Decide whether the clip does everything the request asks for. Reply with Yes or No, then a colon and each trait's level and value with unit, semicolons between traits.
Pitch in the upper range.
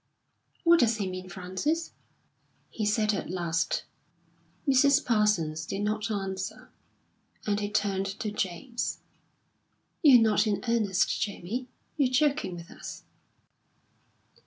Yes: high, 210 Hz